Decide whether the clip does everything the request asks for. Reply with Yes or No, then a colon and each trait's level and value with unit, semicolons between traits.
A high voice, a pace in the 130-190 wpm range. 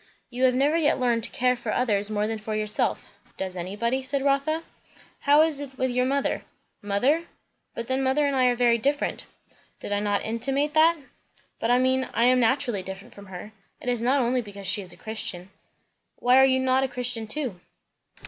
No: very high, 250 Hz; fast, 205 wpm